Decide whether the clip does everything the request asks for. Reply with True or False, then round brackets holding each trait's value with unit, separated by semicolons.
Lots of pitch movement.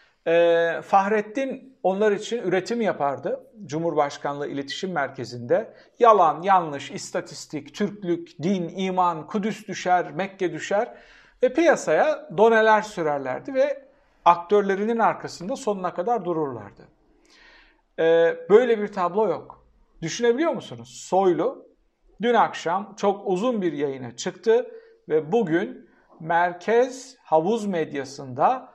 True (6.4 semitones)